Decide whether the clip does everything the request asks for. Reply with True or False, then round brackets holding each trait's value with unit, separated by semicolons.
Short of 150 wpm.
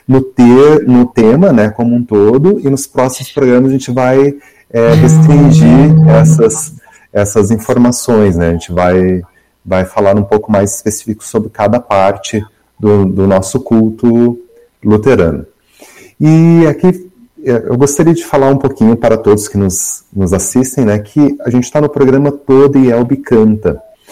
False (155 wpm)